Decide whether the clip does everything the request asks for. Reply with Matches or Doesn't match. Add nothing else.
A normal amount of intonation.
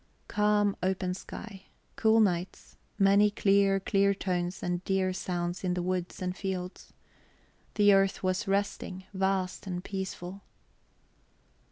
Doesn't match